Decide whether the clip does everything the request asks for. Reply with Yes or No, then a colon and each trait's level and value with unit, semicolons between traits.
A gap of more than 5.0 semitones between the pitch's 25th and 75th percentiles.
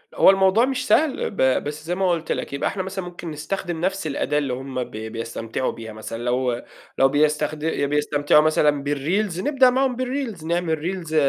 Yes: wide, 5.4 semitones